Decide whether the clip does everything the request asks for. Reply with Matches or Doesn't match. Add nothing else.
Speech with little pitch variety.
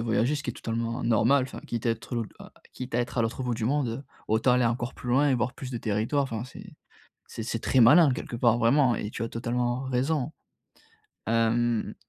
Matches